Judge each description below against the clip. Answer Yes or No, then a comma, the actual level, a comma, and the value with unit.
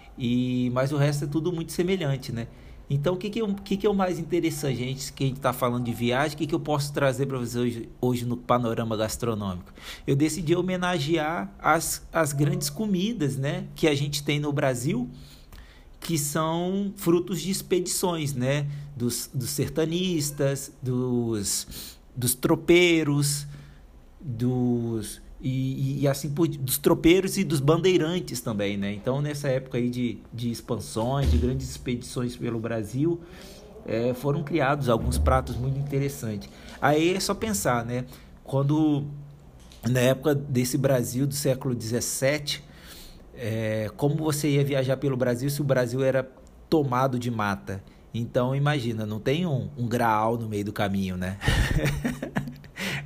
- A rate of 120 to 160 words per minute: Yes, average, 155 wpm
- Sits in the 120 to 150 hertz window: Yes, low, 135 Hz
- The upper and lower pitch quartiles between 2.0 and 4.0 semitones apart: No, average, 4.5 semitones